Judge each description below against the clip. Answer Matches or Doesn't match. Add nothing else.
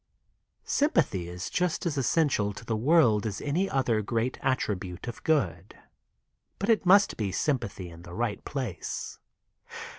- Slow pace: Doesn't match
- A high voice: Doesn't match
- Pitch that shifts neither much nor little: Doesn't match